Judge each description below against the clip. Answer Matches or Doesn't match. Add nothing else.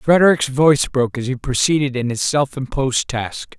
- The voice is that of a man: Matches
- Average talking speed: Matches